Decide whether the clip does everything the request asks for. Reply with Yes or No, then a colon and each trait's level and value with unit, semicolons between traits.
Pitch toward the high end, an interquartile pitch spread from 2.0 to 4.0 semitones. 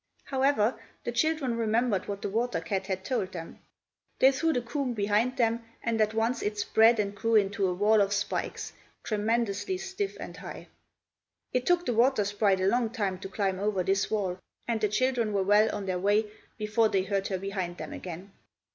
Yes: high, 215 Hz; average, 3.3 semitones